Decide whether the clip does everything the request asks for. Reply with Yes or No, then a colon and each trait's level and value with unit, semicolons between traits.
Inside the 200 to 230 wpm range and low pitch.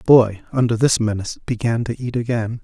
Yes: fast, 205 wpm; low, 115 Hz